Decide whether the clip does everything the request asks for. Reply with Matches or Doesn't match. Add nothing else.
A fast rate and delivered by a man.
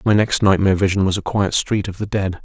Matches